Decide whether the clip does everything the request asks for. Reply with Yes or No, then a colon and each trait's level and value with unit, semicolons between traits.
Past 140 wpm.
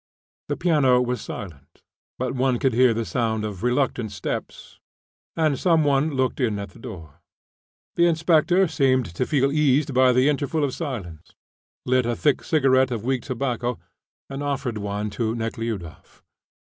Yes: average, 160 wpm